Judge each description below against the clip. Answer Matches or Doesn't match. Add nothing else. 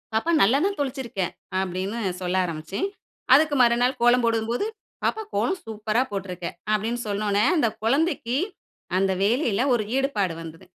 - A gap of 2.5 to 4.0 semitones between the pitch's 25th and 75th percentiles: Doesn't match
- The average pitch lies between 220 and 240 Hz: Matches